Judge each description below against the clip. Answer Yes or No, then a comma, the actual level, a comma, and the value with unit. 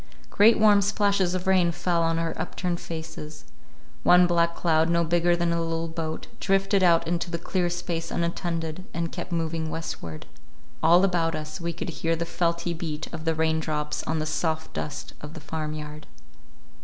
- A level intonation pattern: Yes, narrow, 1.5 semitones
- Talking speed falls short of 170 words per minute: No, average, 175 wpm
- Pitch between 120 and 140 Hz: No, medium, 170 Hz